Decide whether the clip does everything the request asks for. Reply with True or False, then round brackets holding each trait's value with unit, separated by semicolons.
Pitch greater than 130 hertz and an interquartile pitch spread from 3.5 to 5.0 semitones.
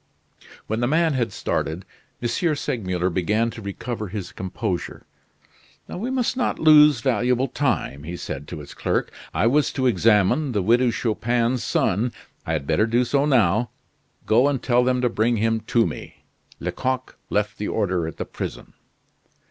False (115 Hz; 4.2 semitones)